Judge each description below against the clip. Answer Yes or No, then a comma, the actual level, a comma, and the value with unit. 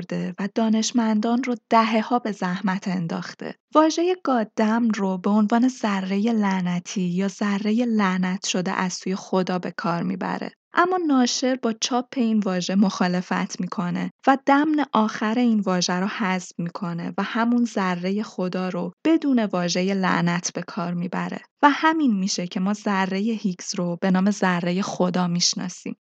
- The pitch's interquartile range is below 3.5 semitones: No, average, 4.0 semitones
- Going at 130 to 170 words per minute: Yes, average, 150 wpm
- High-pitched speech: Yes, high, 200 Hz